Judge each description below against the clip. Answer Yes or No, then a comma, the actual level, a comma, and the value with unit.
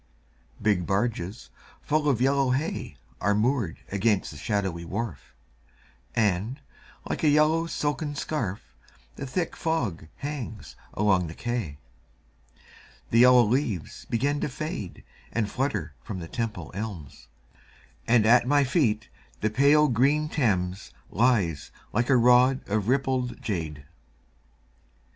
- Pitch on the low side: Yes, low, 115 Hz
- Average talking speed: No, slow, 125 wpm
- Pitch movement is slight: No, wide, 5.6 semitones